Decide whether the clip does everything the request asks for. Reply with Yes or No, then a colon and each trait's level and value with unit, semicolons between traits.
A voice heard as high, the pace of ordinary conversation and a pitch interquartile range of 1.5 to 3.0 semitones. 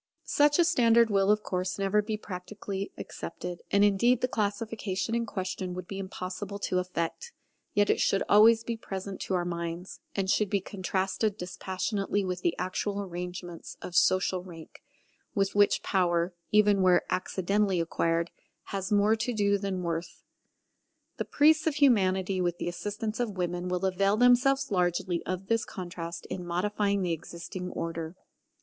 Yes: high, 195 Hz; average, 160 wpm; average, 2.7 semitones